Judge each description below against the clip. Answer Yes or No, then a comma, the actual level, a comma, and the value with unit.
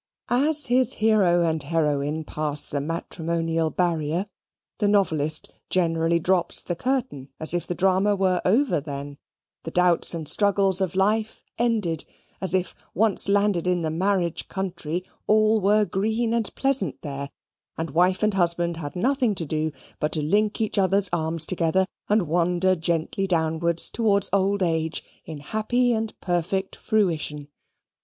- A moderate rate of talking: Yes, average, 150 wpm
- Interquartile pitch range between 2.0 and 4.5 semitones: Yes, average, 3.9 semitones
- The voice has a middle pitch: Yes, medium, 180 Hz